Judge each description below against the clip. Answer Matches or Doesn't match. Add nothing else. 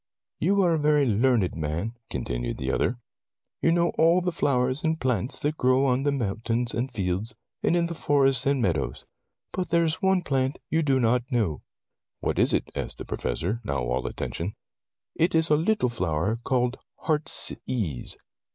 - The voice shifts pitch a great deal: Matches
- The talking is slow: Doesn't match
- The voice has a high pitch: Doesn't match